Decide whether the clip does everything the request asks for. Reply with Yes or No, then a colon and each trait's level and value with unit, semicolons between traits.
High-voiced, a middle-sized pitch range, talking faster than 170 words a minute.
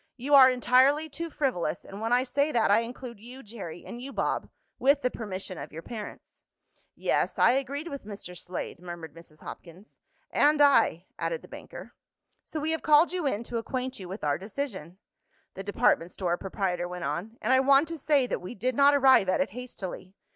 No: high, 240 Hz; wide, 6.8 semitones; average, 200 wpm